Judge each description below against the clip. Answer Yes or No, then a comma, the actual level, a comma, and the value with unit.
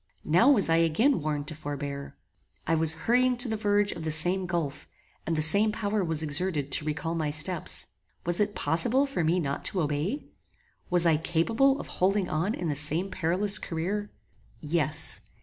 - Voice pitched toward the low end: No, medium, 170 Hz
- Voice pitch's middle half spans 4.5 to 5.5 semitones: Yes, average, 4.8 semitones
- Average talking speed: Yes, average, 185 wpm